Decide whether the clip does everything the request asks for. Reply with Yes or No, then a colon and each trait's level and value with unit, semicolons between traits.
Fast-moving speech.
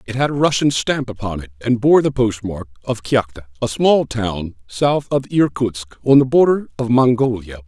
No: average, 190 wpm